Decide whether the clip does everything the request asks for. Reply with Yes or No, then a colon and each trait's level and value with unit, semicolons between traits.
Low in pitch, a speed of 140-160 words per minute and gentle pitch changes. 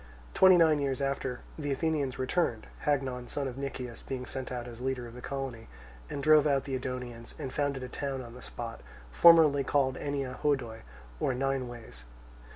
No: low, 130 Hz; average, 180 wpm; narrow, 2.3 semitones